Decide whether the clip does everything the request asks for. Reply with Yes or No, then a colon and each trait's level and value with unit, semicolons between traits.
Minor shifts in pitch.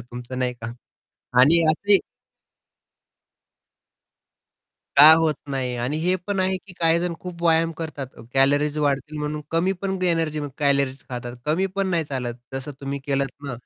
No: average, 3.7 semitones